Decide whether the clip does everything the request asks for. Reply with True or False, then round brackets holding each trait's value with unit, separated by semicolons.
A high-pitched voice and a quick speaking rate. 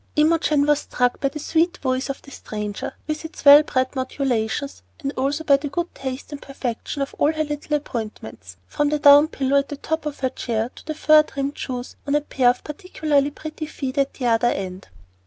True (280 Hz; 210 wpm)